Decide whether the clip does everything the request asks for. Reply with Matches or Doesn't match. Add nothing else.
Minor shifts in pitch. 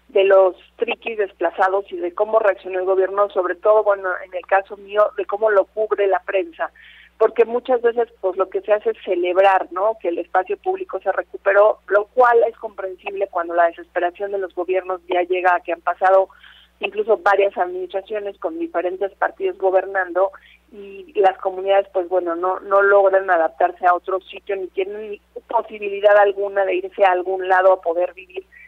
Matches